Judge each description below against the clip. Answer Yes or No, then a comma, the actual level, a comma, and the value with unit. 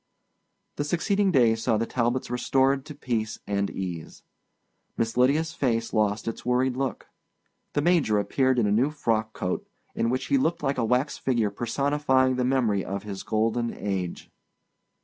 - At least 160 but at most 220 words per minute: Yes, average, 165 wpm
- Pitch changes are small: No, average, 3.8 semitones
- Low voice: Yes, low, 125 Hz